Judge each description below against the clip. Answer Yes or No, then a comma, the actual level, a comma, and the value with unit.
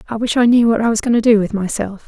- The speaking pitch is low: No, high, 220 Hz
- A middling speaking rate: No, fast, 345 wpm